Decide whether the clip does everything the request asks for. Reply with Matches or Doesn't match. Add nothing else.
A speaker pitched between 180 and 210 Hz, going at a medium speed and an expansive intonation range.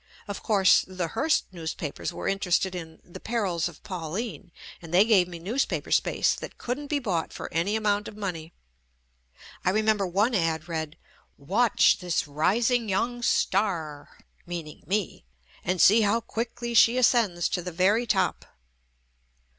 Doesn't match